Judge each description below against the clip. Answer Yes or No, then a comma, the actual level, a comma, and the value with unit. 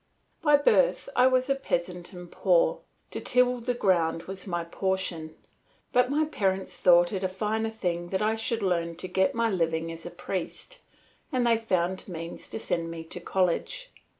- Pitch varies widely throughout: Yes, wide, 5.8 semitones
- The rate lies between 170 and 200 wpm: Yes, average, 180 wpm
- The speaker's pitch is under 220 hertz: Yes, high, 190 Hz